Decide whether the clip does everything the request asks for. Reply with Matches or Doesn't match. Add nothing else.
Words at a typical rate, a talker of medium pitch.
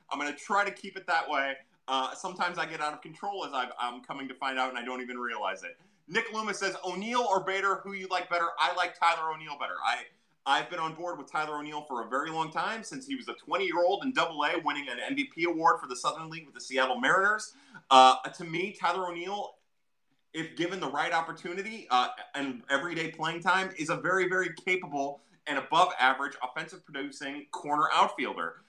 Doesn't match